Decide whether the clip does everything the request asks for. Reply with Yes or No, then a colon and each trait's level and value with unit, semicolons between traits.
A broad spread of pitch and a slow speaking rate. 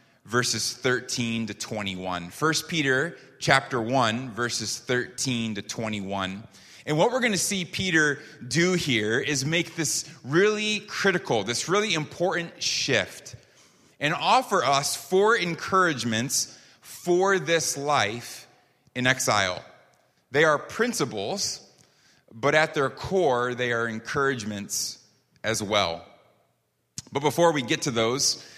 Yes: wide, 6.3 semitones; slow, 120 wpm